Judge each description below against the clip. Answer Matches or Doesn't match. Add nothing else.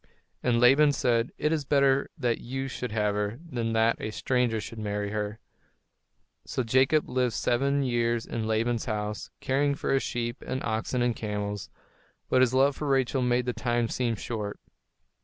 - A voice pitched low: Matches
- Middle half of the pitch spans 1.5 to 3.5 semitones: Matches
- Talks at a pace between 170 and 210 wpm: Matches